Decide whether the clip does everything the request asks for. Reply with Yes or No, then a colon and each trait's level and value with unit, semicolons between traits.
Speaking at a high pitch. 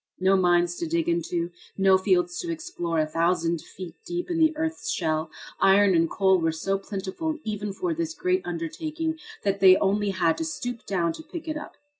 Yes: high, 195 Hz